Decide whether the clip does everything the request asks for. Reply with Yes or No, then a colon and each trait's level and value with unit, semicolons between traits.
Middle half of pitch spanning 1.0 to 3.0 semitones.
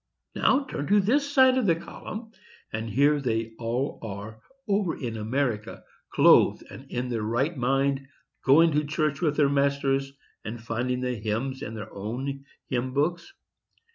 No: average, 4.6 semitones